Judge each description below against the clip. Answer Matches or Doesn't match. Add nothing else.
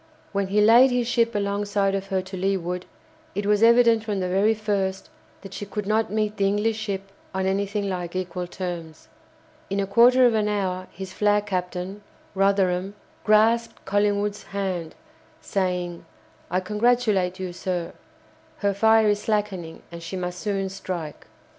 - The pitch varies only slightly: Matches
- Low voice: Doesn't match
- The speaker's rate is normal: Matches